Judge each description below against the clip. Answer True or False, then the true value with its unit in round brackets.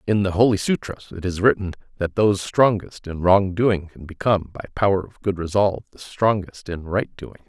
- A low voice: True (95 Hz)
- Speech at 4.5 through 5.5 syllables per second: True (5.4 syllables/s)